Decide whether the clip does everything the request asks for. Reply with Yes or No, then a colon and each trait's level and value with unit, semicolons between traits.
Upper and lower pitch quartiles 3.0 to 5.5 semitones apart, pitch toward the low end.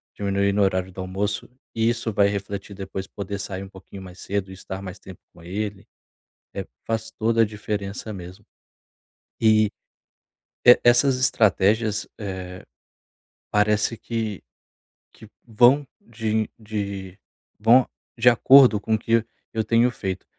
No: narrow, 2.6 semitones; low, 105 Hz